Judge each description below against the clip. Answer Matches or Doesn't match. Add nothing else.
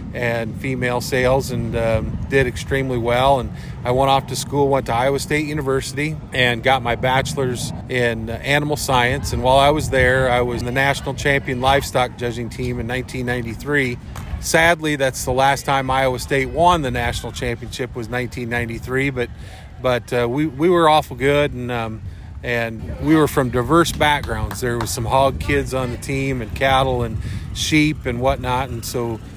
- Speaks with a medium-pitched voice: Doesn't match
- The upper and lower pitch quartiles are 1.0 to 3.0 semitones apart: Matches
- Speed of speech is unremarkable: Matches